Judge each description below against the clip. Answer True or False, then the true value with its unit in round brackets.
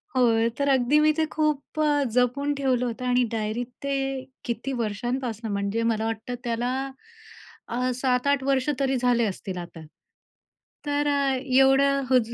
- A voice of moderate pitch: False (250 Hz)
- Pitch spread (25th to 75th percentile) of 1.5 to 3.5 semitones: True (3.2 semitones)